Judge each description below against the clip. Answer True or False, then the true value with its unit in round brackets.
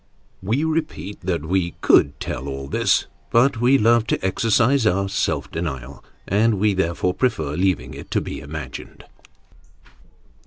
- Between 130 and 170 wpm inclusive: True (145 wpm)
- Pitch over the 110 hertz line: False (95 Hz)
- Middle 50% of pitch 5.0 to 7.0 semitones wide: True (5.4 semitones)